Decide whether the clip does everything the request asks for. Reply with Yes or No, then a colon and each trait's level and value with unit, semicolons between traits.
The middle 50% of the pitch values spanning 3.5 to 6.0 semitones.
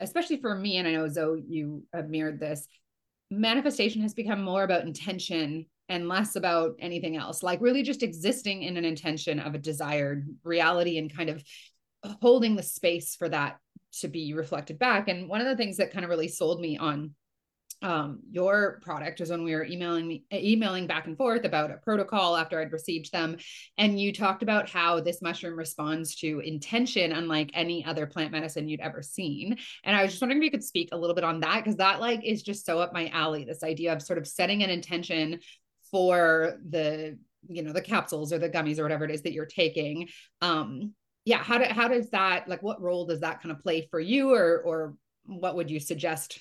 Yes: average, 3.9 semitones